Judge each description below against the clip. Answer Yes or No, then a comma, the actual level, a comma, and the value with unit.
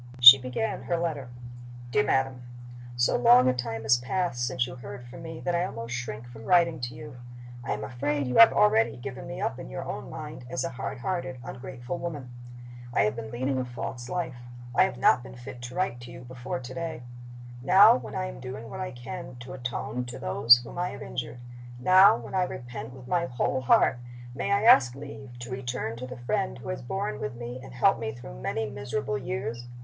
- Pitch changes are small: Yes, narrow, 2.2 semitones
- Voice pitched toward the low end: Yes, low, 125 Hz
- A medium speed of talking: No, fast, 215 wpm